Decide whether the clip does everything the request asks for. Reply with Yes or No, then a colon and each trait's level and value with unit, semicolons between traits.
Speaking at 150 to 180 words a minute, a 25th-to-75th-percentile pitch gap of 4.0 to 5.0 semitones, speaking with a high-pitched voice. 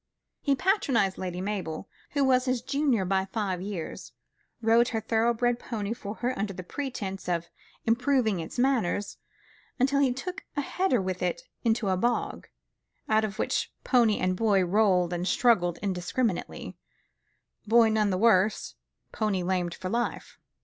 Yes: average, 155 wpm; average, 4.6 semitones; high, 220 Hz